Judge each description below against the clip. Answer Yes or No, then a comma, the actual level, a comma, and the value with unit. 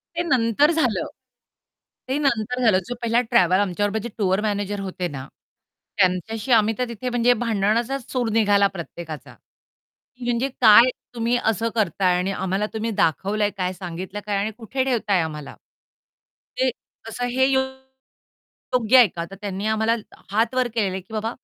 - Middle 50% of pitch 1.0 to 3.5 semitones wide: No, average, 3.9 semitones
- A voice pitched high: Yes, high, 220 Hz